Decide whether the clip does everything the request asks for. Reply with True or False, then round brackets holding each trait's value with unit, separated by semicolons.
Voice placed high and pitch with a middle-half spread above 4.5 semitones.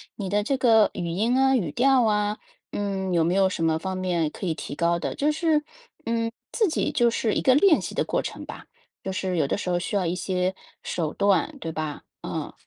True (195 Hz; 5.4 semitones)